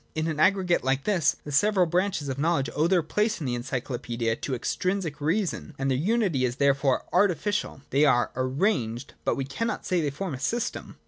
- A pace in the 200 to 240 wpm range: Yes, fast, 205 wpm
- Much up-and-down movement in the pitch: Yes, wide, 5.8 semitones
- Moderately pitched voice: Yes, medium, 150 Hz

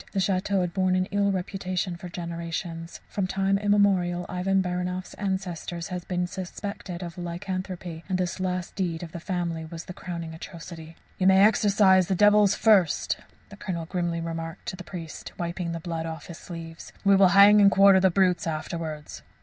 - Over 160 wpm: Yes, average, 180 wpm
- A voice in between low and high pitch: Yes, medium, 180 Hz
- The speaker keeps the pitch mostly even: Yes, narrow, 2.3 semitones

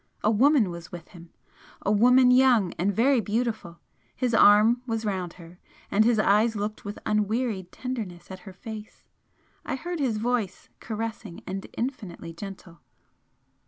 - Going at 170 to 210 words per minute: No, average, 150 wpm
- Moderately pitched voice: No, high, 215 Hz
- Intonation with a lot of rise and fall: No, average, 4.1 semitones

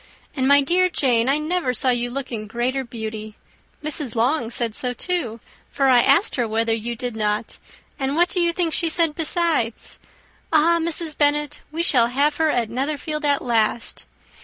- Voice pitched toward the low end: No, very high, 270 Hz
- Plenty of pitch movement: No, average, 4.9 semitones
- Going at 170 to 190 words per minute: Yes, average, 185 wpm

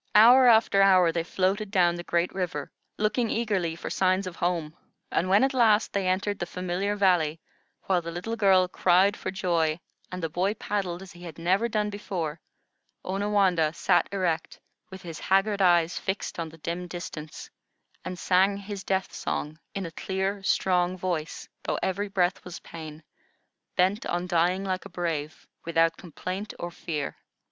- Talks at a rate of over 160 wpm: Yes, average, 170 wpm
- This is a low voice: No, medium, 185 Hz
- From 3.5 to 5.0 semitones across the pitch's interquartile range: No, narrow, 2.6 semitones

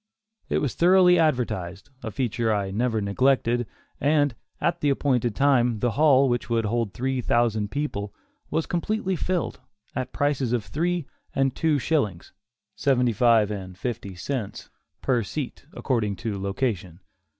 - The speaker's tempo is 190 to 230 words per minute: No, average, 145 wpm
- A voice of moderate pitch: No, low, 125 Hz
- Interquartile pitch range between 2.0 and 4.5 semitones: No, average, 5.0 semitones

